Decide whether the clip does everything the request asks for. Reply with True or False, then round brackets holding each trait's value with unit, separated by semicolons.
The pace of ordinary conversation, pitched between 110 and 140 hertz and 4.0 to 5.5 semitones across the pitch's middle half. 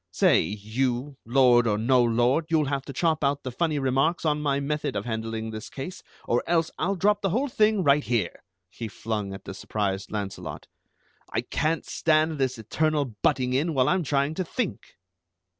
True (185 wpm; 135 Hz; 5.2 semitones)